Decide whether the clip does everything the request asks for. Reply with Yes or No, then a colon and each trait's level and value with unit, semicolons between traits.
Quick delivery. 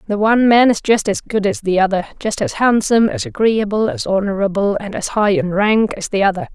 Yes: fast, 230 wpm